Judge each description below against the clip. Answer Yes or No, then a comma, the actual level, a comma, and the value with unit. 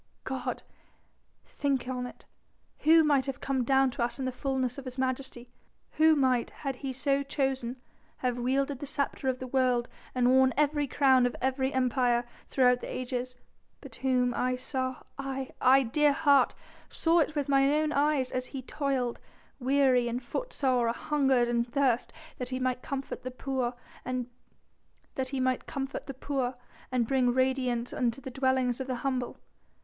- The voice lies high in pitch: Yes, very high, 260 Hz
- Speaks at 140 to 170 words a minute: Yes, average, 155 wpm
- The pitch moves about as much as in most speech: No, narrow, 1.6 semitones